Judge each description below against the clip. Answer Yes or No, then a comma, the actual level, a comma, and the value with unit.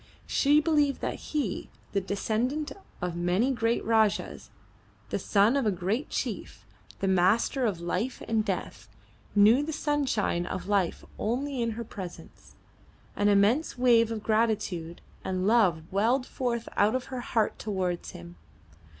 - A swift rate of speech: No, average, 145 wpm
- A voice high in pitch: Yes, high, 220 Hz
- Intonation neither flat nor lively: Yes, average, 4.6 semitones